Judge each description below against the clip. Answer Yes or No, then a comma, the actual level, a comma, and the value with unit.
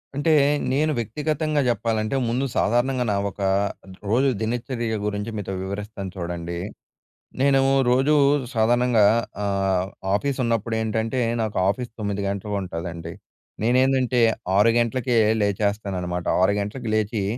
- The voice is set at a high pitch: No, low, 110 Hz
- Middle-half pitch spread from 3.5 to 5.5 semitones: Yes, average, 3.8 semitones